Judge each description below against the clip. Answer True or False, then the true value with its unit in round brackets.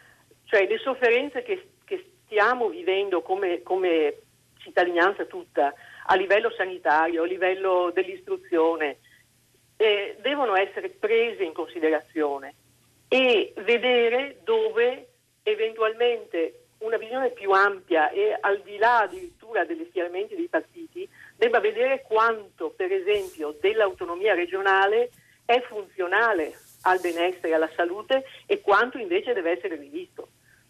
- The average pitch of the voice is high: True (245 Hz)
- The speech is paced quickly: False (115 wpm)